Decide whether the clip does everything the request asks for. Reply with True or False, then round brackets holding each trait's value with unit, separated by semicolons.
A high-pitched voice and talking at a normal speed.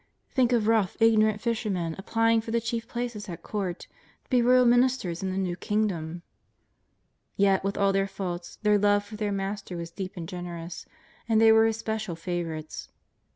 True (205 Hz; 185 wpm)